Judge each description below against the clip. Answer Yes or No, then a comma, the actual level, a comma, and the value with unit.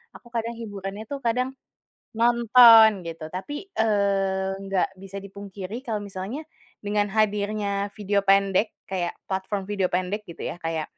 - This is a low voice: No, high, 200 Hz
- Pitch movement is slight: Yes, narrow, 2.3 semitones